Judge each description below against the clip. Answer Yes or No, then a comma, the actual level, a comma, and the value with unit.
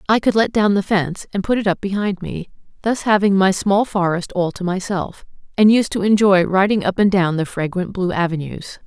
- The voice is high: Yes, high, 195 Hz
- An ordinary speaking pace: No, fast, 215 wpm